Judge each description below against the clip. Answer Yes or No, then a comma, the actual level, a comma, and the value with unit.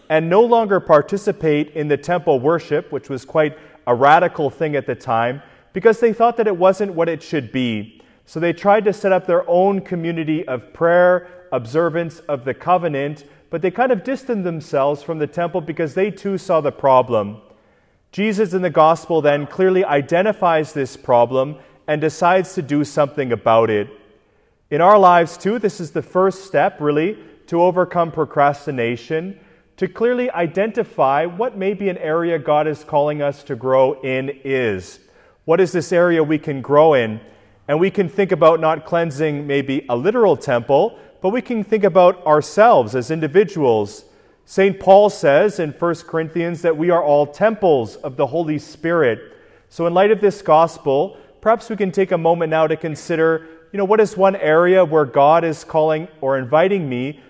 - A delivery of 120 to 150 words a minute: No, average, 180 wpm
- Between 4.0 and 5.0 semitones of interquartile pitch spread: Yes, average, 4.4 semitones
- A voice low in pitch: No, medium, 165 Hz